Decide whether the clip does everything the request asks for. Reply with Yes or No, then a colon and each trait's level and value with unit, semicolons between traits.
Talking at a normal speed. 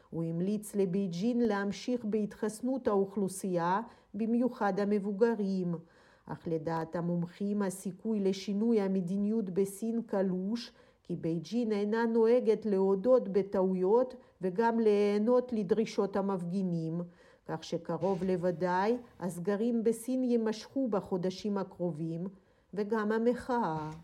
No: slow, 90 wpm